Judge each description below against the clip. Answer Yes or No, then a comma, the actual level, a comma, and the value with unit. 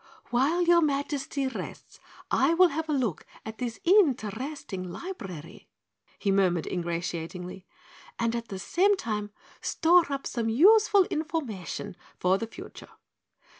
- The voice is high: Yes, high, 245 Hz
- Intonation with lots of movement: Yes, wide, 8.9 semitones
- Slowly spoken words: Yes, slow, 130 wpm